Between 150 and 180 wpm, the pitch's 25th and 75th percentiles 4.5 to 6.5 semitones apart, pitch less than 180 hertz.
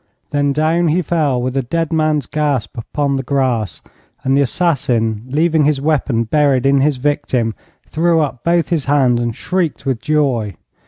No: average, 170 wpm; average, 3.6 semitones; medium, 140 Hz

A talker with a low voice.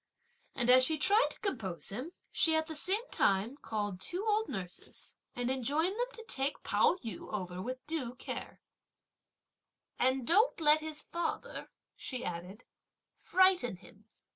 No: very high, 270 Hz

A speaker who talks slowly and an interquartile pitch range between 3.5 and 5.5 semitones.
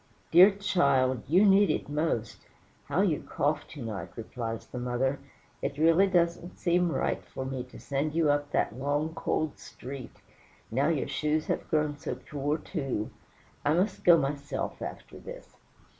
No: average, 160 wpm; average, 4.1 semitones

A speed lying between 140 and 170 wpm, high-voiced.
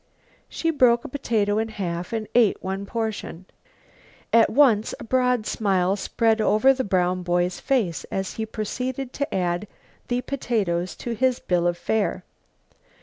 Yes: average, 150 wpm; high, 215 Hz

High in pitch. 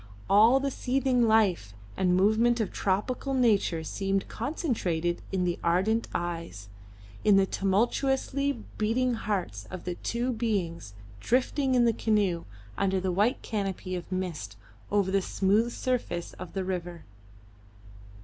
Yes: high, 200 Hz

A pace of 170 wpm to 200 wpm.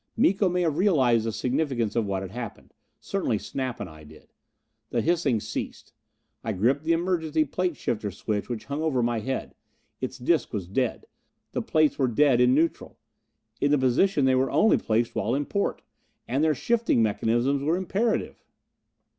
Yes: average, 175 wpm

